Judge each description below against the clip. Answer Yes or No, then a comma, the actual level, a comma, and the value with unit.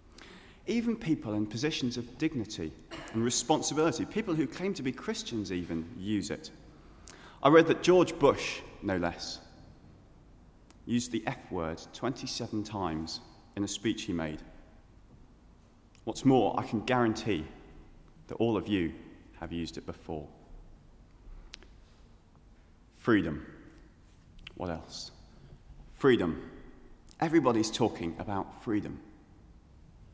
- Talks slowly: Yes, slow, 110 wpm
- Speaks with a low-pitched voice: Yes, low, 110 Hz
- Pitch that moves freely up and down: Yes, wide, 7.1 semitones